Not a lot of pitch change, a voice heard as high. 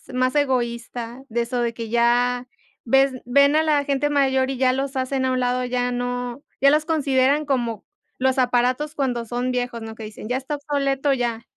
Yes: narrow, 2.2 semitones; very high, 255 Hz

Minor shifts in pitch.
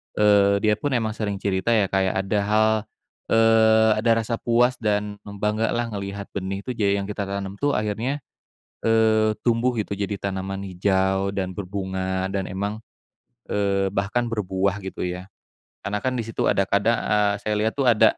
Yes: narrow, 2.2 semitones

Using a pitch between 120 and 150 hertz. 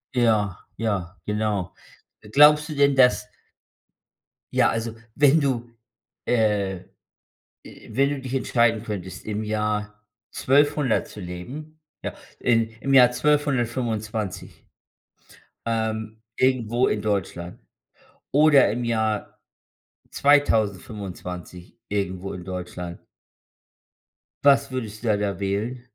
No: low, 110 Hz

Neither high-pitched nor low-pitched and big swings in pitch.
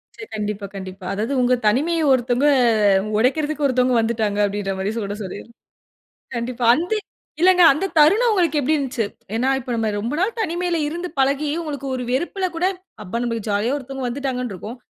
No: very high, 255 Hz; wide, 5.7 semitones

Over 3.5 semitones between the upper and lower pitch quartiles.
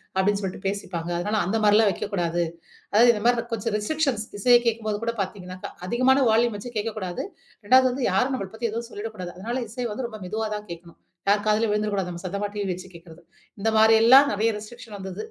No: average, 3.2 semitones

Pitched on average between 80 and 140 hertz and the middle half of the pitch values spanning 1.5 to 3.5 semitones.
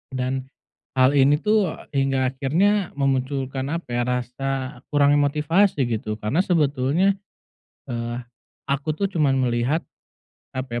Yes: low, 135 Hz; average, 2.9 semitones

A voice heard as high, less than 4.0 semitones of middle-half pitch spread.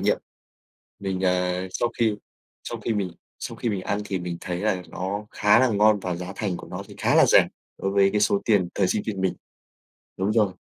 No: very low, 95 Hz; narrow, 2.4 semitones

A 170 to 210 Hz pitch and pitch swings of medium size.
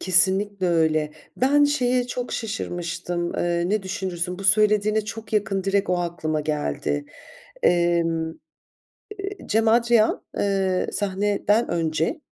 Yes: high, 190 Hz; average, 3.7 semitones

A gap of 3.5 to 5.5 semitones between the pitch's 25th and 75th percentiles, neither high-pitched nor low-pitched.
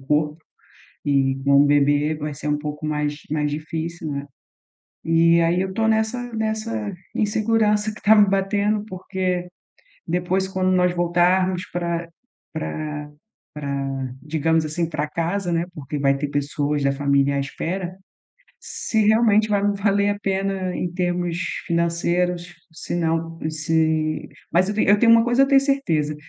Yes: average, 4.7 semitones; medium, 170 Hz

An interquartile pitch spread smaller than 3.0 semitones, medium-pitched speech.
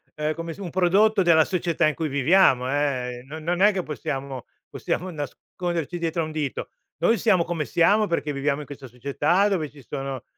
No: average, 4.0 semitones; medium, 155 Hz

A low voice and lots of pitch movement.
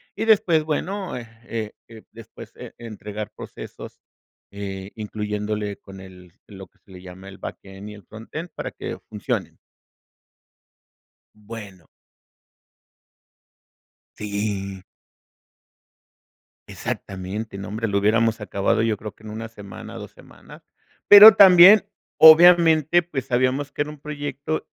Yes: low, 110 Hz; wide, 6.5 semitones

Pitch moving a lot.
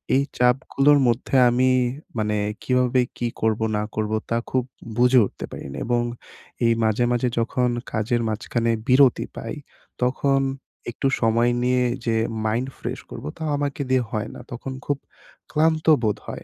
No: narrow, 2.4 semitones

